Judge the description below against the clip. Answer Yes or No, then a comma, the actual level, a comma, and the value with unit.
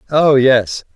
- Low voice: Yes, low, 130 Hz